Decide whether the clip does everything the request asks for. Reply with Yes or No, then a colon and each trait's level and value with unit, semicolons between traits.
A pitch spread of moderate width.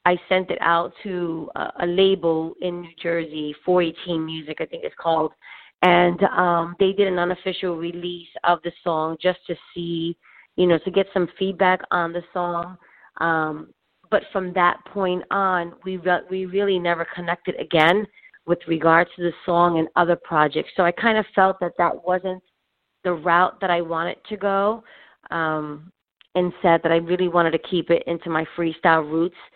No: narrow, 1.7 semitones